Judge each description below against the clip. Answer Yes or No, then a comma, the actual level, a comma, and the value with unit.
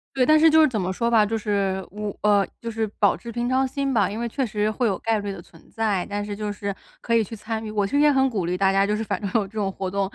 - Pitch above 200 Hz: Yes, high, 210 Hz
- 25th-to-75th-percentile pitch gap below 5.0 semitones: Yes, average, 2.8 semitones